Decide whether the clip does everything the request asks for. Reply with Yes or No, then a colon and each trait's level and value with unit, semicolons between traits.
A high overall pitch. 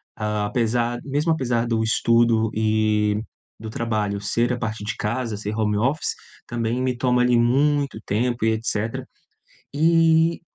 No: low, 115 Hz